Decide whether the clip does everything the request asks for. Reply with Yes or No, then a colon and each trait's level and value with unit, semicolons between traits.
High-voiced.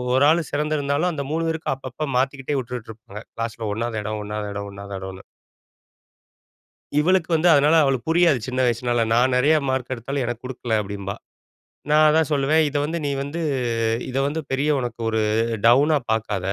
No: low, 130 Hz